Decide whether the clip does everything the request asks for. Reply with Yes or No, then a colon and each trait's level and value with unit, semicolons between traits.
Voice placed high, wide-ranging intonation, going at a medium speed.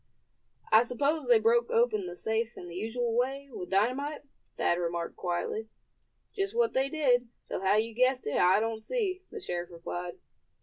Yes: high, 230 Hz; wide, 6.0 semitones; average, 175 wpm